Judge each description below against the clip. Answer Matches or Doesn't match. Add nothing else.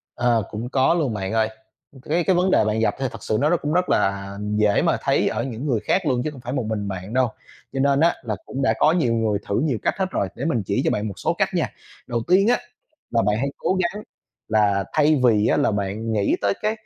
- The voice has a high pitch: Doesn't match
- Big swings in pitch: Matches